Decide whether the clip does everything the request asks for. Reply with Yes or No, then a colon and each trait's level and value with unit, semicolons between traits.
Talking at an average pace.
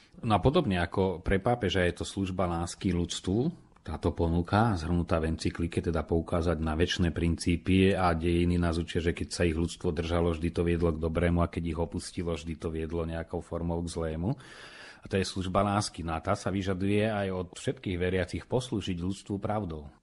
No: fast, 190 wpm